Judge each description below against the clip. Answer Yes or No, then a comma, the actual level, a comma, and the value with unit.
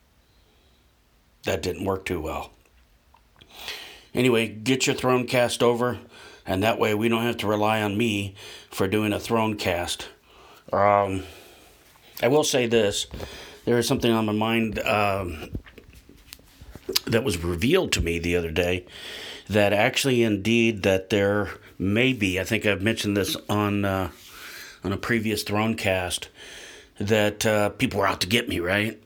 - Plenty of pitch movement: No, average, 3.4 semitones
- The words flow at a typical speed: Yes, average, 155 wpm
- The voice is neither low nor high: No, low, 105 Hz